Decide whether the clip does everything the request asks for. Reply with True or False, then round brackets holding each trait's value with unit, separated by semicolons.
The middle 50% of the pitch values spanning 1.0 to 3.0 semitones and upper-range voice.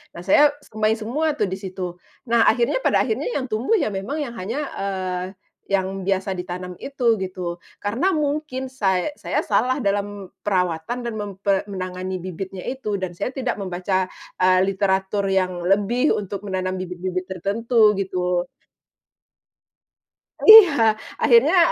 False (4.3 semitones; 195 Hz)